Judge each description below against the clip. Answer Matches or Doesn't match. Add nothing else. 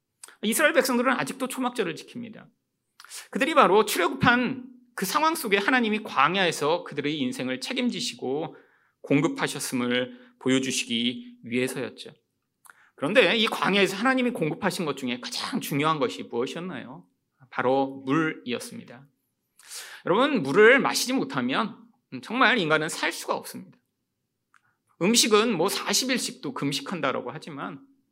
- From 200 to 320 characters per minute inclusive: Matches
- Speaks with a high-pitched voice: Matches